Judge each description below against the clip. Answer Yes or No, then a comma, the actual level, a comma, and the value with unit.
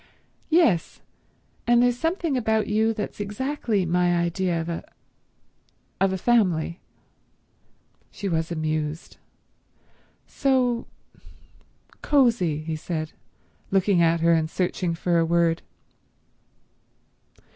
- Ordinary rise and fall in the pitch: No, wide, 5.8 semitones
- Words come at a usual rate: No, slow, 95 wpm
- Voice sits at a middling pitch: Yes, medium, 180 Hz